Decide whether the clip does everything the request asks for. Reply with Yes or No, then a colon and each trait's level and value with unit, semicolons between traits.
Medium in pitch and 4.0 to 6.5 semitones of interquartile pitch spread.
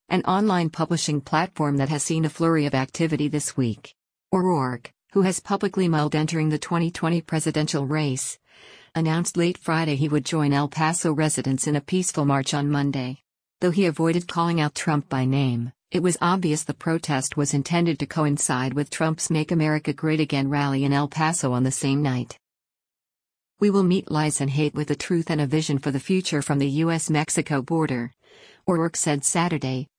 No: medium, 155 Hz; average, 2.8 semitones